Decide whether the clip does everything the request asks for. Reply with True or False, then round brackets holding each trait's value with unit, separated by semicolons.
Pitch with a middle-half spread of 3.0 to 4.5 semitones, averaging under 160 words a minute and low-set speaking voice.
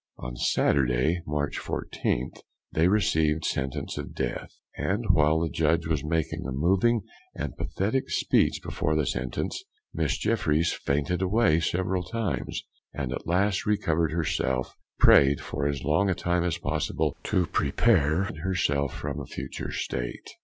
True (4.2 semitones; 145 wpm; 80 Hz)